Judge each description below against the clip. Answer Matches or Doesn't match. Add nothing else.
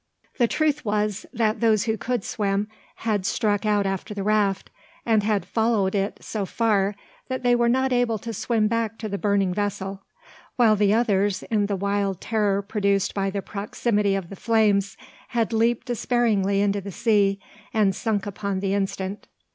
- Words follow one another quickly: Doesn't match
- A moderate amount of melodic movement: Doesn't match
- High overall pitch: Matches